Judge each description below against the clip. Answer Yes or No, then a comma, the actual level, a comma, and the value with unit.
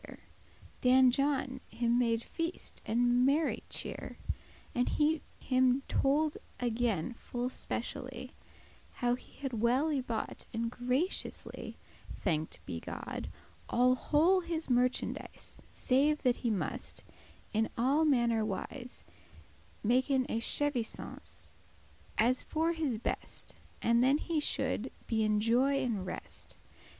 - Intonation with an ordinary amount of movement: Yes, average, 3.2 semitones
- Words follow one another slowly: Yes, slow, 125 wpm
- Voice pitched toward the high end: Yes, very high, 250 Hz